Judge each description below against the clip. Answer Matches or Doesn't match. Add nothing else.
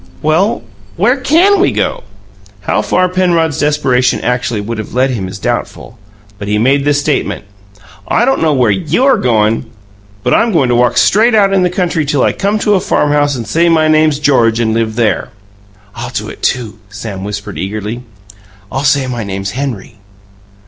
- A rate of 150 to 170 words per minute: Doesn't match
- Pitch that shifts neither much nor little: Doesn't match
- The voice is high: Doesn't match